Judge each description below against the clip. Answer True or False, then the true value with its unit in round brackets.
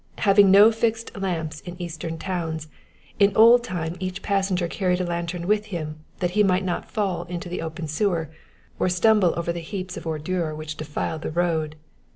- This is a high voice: False (175 Hz)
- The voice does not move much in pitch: False (3.2 semitones)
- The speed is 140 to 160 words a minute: False (185 wpm)